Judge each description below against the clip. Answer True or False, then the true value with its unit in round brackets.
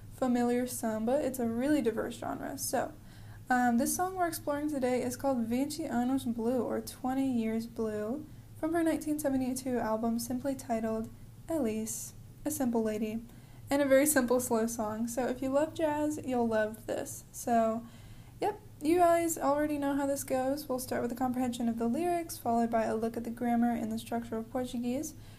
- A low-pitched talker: False (250 Hz)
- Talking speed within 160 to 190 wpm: True (180 wpm)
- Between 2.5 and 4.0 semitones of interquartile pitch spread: True (3.3 semitones)